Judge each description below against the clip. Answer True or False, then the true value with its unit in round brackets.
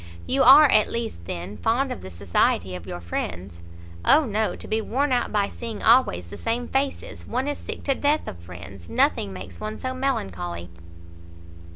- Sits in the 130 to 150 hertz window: False (215 Hz)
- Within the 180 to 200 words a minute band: True (185 wpm)